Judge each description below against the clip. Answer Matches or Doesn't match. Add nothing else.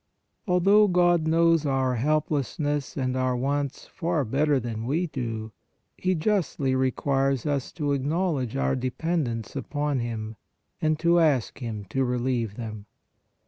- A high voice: Doesn't match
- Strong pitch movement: Doesn't match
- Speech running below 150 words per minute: Matches